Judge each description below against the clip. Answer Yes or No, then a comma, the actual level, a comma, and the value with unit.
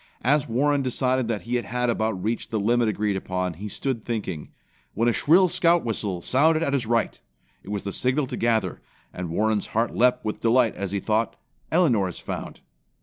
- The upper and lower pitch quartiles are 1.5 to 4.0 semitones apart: Yes, average, 3.7 semitones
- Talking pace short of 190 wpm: No, average, 195 wpm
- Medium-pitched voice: No, low, 115 Hz